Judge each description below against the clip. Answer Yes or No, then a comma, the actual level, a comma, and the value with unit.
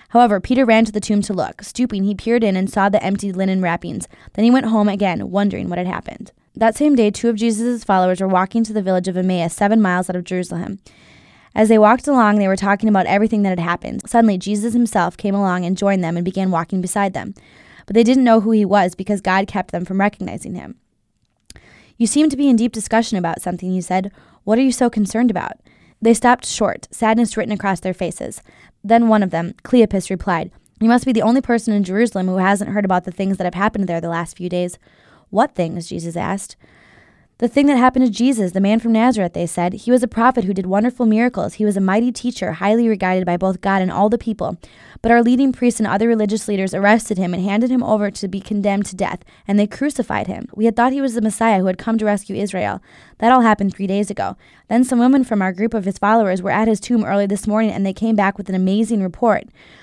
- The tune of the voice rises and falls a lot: No, average, 3.2 semitones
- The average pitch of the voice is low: No, high, 205 Hz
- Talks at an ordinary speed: No, fast, 245 wpm